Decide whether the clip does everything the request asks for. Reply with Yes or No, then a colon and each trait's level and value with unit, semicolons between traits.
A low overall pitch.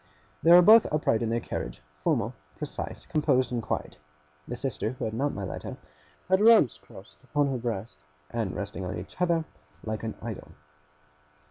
Yes: low, 120 Hz